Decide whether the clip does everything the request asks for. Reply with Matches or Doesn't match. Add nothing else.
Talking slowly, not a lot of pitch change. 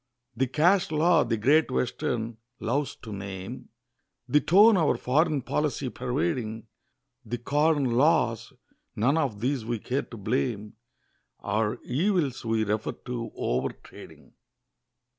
Doesn't match